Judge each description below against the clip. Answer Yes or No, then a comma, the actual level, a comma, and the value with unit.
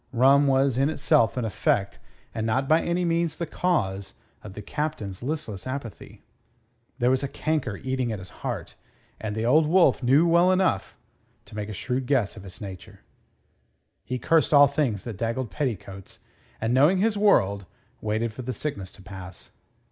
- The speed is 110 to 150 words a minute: No, average, 170 wpm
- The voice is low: Yes, low, 125 Hz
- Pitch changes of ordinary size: No, wide, 6.1 semitones